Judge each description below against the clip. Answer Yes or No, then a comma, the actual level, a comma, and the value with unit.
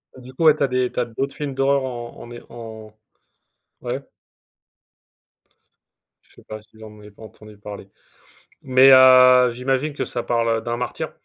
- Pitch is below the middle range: Yes, low, 125 Hz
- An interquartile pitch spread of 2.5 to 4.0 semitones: Yes, average, 2.8 semitones